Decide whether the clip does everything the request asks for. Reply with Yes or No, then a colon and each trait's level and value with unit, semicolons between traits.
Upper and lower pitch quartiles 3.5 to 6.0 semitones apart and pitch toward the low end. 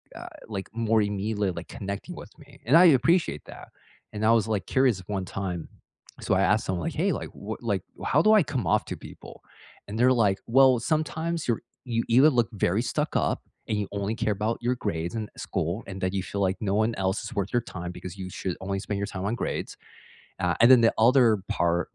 Yes: average, 4.1 semitones; low, 105 Hz